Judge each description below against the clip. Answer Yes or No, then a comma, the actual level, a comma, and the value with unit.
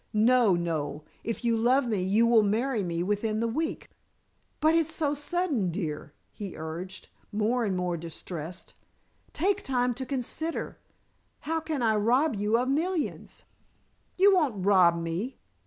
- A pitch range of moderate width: No, wide, 7.0 semitones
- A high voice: Yes, high, 225 Hz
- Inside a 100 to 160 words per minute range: Yes, average, 150 wpm